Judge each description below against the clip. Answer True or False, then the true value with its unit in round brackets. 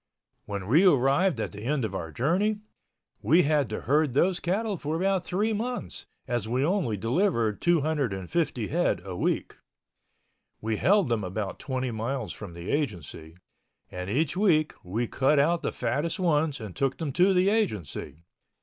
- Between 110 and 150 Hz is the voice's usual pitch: True (140 Hz)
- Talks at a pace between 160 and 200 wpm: True (165 wpm)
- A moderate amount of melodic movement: False (8.2 semitones)